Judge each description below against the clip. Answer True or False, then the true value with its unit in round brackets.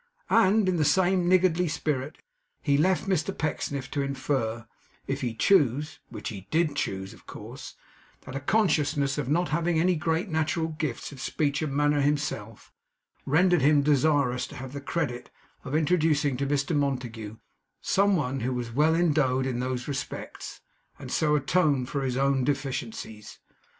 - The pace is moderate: True (160 wpm)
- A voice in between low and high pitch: True (145 Hz)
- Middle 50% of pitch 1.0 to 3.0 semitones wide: False (3.6 semitones)